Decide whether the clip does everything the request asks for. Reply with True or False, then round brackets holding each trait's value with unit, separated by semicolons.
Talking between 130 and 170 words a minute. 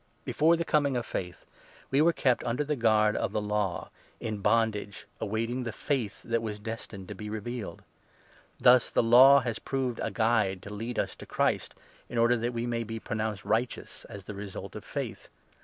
False (200 wpm)